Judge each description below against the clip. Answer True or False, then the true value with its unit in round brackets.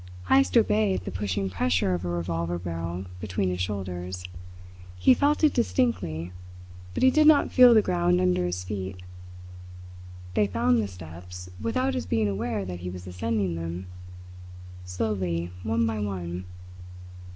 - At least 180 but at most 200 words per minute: False (150 wpm)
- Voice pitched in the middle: False (90 Hz)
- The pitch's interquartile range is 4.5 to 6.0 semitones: False (3.3 semitones)